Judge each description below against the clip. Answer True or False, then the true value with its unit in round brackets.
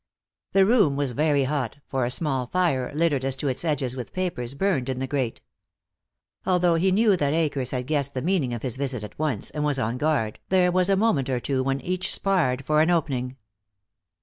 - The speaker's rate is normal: False (210 wpm)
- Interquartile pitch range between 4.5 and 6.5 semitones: True (5.0 semitones)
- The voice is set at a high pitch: False (140 Hz)